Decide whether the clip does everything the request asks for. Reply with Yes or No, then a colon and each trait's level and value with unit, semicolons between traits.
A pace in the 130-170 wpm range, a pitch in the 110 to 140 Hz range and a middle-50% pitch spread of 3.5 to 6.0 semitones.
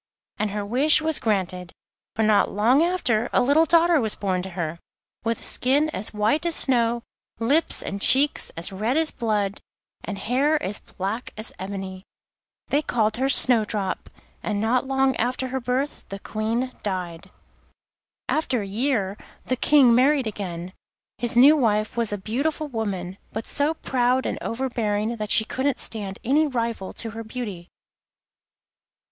No: average, 160 wpm; high, 230 Hz; average, 4.5 semitones